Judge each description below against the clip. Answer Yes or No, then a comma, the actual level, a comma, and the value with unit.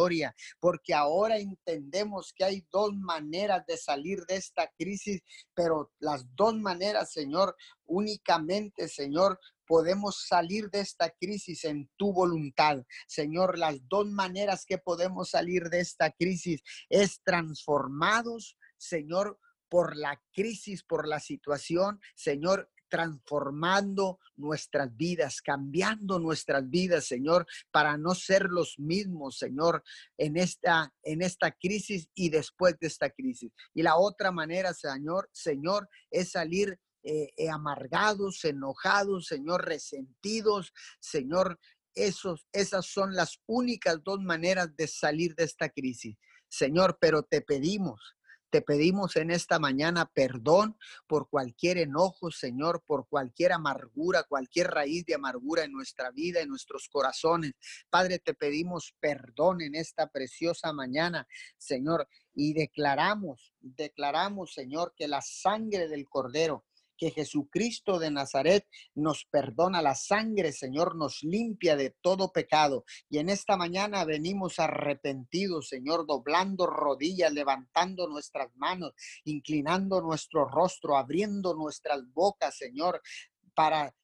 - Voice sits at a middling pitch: Yes, medium, 170 Hz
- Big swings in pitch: No, average, 4.1 semitones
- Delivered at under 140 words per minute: Yes, slow, 125 wpm